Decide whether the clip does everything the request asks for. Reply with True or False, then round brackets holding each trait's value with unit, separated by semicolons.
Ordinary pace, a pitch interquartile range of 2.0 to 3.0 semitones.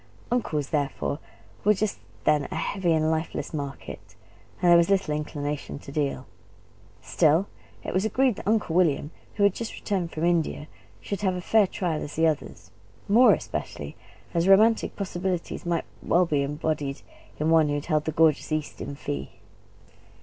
False (170 wpm; 4.2 semitones)